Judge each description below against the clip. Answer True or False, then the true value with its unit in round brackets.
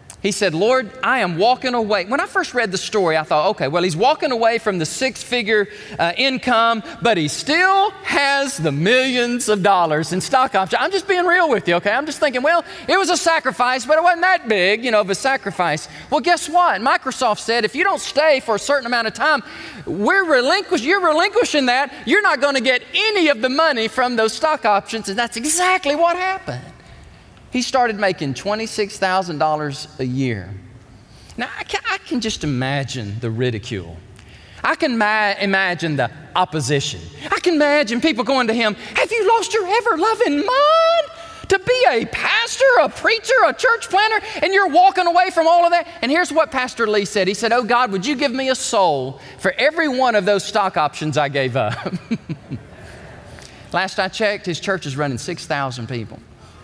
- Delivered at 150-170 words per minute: False (195 wpm)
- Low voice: False (240 Hz)